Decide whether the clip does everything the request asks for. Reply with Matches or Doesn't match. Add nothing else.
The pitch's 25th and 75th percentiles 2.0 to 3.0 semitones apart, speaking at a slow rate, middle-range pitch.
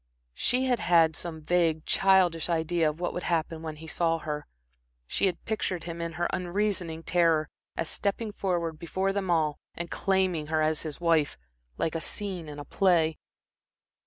Doesn't match